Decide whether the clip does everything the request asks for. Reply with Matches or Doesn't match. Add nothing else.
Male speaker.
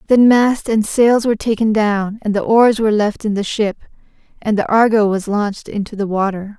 Doesn't match